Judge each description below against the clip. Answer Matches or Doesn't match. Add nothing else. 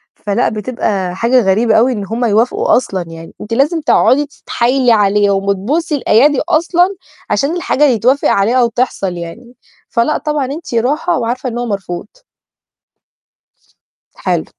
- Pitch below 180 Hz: Doesn't match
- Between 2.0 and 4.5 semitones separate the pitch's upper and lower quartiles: Doesn't match